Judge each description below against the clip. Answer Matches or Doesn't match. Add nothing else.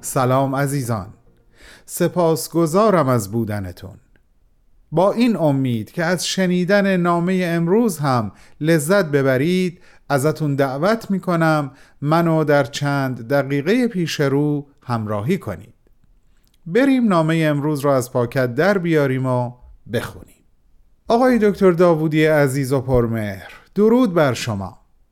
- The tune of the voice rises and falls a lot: Matches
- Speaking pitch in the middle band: Matches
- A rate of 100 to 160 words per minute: Matches